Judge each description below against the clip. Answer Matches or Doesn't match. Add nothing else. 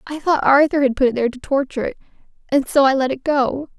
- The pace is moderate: Doesn't match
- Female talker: Matches